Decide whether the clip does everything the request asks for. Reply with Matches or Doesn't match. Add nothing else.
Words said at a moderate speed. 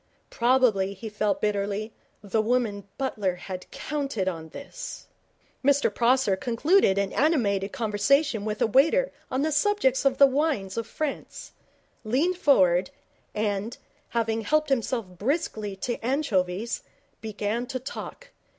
Doesn't match